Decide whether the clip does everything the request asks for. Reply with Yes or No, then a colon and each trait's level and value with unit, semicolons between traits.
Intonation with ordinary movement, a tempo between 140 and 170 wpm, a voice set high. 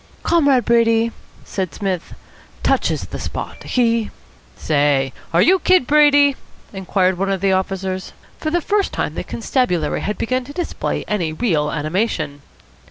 No: wide, 6.4 semitones; average, 150 wpm; high, 205 Hz